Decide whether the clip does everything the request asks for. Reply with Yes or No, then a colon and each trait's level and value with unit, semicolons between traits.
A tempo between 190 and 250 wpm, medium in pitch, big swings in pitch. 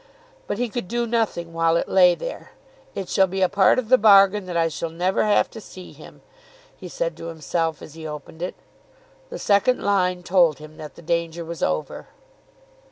No: average, 200 wpm; medium, 180 Hz; average, 3.5 semitones